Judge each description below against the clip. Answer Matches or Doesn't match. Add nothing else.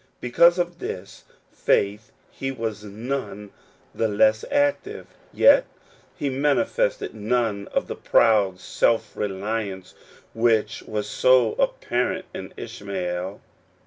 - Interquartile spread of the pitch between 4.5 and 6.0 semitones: Matches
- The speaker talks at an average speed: Doesn't match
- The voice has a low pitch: Matches